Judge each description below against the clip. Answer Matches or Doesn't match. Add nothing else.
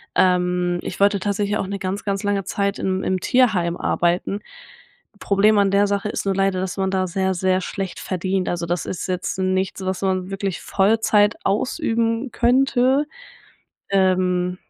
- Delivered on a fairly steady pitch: Matches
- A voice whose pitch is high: Matches